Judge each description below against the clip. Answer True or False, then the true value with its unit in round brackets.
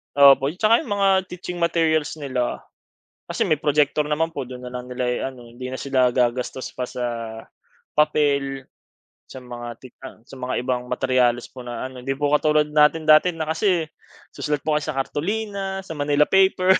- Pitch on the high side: False (145 Hz)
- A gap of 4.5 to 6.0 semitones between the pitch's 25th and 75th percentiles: False (4.0 semitones)